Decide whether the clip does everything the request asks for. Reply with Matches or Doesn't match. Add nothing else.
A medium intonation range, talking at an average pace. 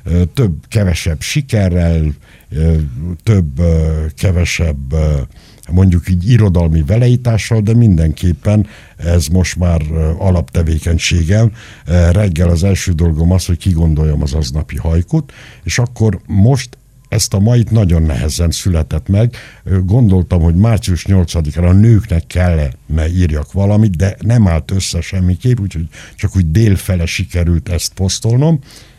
Matches